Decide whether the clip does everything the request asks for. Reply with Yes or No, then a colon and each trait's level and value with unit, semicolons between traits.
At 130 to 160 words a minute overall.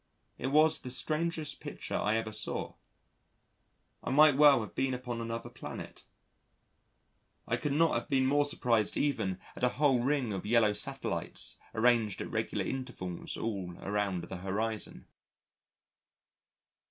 Yes: average, 140 wpm